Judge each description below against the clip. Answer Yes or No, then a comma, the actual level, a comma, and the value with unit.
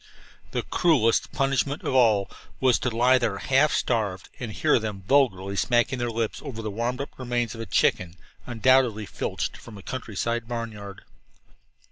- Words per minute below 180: Yes, average, 160 wpm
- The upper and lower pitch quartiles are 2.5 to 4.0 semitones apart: Yes, average, 3.2 semitones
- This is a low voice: Yes, low, 115 Hz